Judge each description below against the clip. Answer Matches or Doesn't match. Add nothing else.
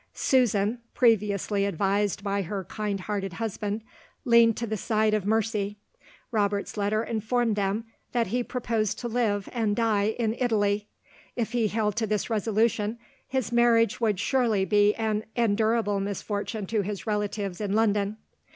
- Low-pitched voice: Doesn't match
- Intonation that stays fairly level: Matches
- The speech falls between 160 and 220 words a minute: Doesn't match